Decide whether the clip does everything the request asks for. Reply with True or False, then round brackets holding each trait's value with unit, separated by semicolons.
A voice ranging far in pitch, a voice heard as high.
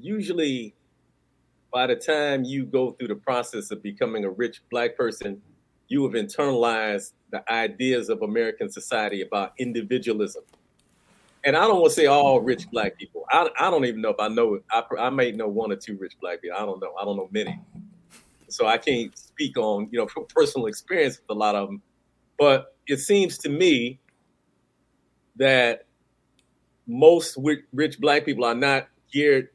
False (8.9 semitones; 140 Hz)